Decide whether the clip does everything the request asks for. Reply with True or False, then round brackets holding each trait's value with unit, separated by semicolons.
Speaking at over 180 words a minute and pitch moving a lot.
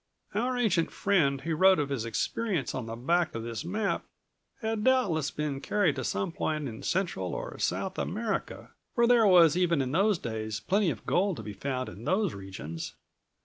True (190 wpm; 8.0 semitones)